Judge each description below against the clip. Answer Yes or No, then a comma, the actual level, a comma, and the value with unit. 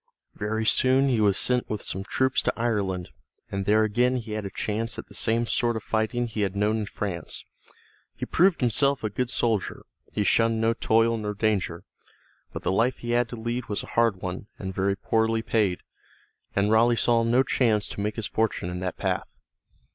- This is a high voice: No, low, 110 Hz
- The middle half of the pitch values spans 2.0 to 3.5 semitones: Yes, narrow, 2.5 semitones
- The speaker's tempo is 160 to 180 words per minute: No, average, 200 wpm